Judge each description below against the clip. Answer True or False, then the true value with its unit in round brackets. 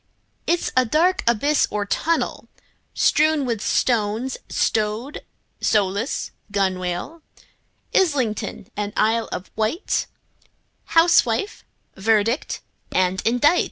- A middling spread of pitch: False (6.2 semitones)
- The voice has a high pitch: True (230 Hz)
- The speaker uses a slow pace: True (90 wpm)